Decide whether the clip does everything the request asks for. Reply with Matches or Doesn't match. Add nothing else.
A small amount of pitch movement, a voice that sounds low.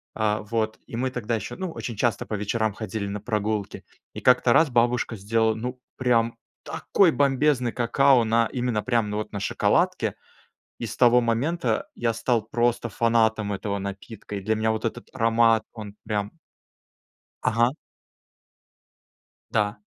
Matches